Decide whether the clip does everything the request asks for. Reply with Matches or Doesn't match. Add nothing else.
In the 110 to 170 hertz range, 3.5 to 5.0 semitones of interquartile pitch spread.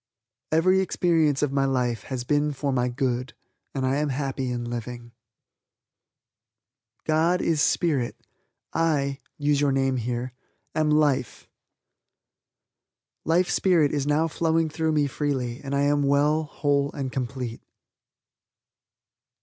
Doesn't match